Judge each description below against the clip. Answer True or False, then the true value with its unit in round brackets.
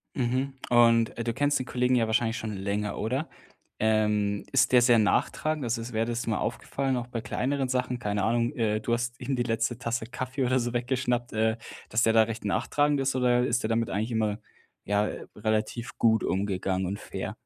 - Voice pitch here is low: True (115 Hz)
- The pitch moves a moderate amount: False (2.3 semitones)